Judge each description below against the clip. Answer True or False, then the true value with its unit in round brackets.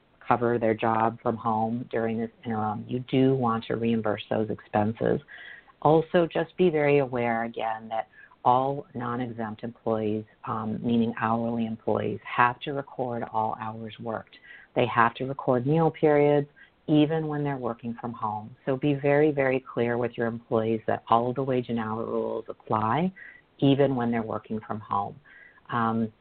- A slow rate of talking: False (165 wpm)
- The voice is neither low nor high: False (115 Hz)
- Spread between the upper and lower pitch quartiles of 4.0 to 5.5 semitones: False (2.9 semitones)